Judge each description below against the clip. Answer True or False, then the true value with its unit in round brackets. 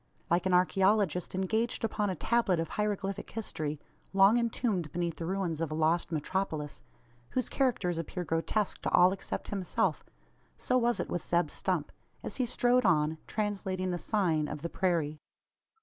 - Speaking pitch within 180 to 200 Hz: True (185 Hz)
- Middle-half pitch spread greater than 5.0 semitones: False (4.2 semitones)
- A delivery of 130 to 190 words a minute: True (165 wpm)